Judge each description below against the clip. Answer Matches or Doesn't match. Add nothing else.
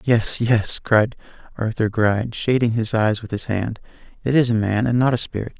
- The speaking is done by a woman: Doesn't match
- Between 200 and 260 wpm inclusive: Matches